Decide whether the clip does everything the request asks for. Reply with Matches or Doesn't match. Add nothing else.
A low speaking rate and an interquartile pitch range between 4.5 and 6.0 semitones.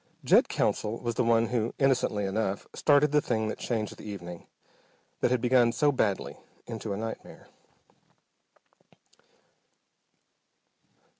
Doesn't match